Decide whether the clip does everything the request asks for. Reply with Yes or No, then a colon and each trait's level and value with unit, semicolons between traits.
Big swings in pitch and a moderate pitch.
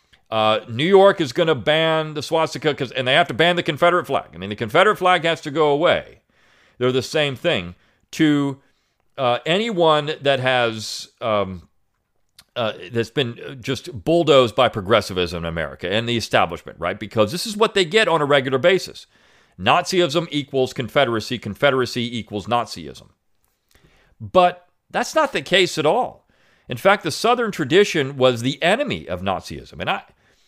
Yes: wide, 6.6 semitones; medium, 145 Hz